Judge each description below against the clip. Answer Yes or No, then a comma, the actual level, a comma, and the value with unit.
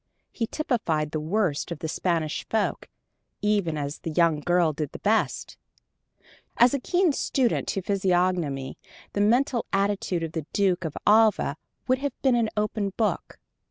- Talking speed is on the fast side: No, average, 160 wpm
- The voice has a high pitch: Yes, high, 195 Hz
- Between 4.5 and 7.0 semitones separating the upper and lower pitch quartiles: Yes, wide, 5.5 semitones